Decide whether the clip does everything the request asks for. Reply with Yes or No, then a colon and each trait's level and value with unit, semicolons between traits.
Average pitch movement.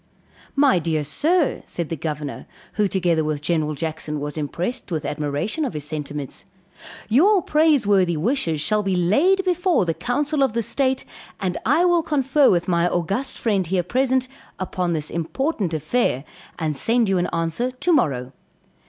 No: wide, 9.0 semitones